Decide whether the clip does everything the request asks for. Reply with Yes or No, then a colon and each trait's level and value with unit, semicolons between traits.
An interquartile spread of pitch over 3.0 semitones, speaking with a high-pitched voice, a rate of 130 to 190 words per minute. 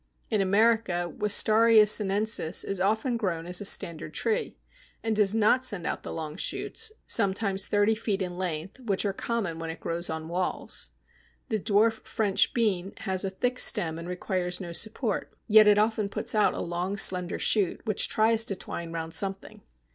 Yes: average, 3.6 semitones; high, 200 Hz; average, 175 wpm